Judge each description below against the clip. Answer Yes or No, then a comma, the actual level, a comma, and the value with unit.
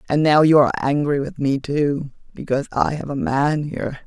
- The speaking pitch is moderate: Yes, medium, 145 Hz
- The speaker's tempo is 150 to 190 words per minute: No, fast, 205 wpm